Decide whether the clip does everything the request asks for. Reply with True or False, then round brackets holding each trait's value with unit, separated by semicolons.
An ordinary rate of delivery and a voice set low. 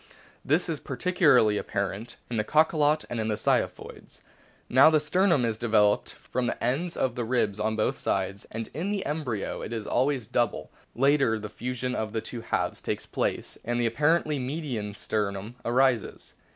True (180 wpm; 120 Hz)